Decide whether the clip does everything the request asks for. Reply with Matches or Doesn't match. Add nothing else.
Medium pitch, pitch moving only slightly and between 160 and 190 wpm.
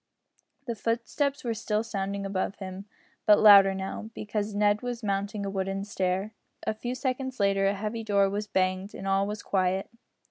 Doesn't match